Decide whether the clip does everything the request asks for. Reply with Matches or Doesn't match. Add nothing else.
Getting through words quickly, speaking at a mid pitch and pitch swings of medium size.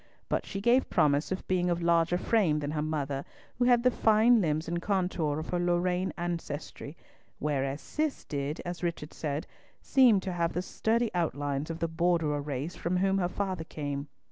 Doesn't match